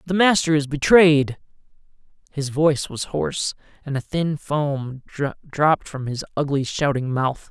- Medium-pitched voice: Yes, medium, 145 Hz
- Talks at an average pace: Yes, average, 145 wpm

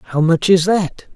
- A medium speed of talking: No, fast, 210 wpm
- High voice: No, medium, 175 Hz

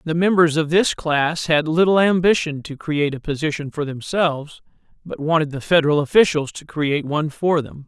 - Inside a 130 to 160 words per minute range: No, average, 185 wpm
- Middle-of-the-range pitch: Yes, medium, 155 Hz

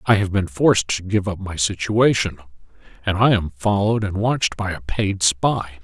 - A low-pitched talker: Yes, low, 100 Hz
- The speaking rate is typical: Yes, average, 195 wpm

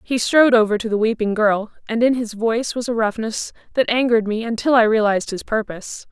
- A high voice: Yes, high, 225 Hz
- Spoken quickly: Yes, fast, 215 wpm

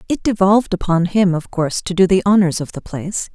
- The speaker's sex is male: No, female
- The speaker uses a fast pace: Yes, fast, 235 wpm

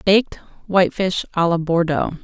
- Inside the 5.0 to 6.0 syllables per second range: Yes, 5.6 syllables/s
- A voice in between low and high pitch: Yes, medium, 180 Hz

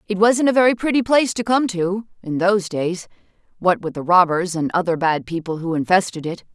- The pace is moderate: No, fast, 210 wpm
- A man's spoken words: No, female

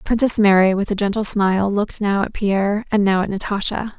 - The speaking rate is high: Yes, fast, 210 wpm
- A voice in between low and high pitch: No, high, 200 Hz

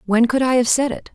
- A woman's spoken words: Yes, female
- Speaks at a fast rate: Yes, fast, 315 wpm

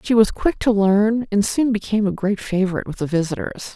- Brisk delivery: Yes, fast, 225 wpm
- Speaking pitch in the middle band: No, high, 205 Hz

